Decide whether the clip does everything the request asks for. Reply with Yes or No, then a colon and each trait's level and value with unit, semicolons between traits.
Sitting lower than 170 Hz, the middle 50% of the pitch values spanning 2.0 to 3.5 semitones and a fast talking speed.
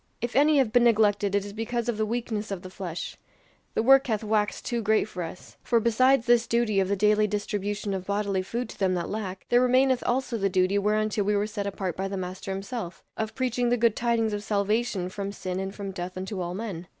No: high, 210 Hz; average, 3.2 semitones; fast, 235 wpm